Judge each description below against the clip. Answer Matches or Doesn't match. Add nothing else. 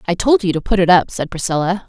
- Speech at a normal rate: Doesn't match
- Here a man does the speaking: Doesn't match